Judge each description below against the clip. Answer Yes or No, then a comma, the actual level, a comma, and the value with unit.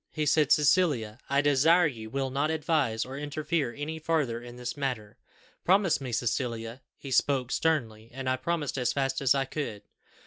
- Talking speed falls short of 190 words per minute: Yes, average, 175 wpm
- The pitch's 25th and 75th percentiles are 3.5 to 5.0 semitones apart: Yes, average, 3.9 semitones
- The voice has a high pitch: No, low, 135 Hz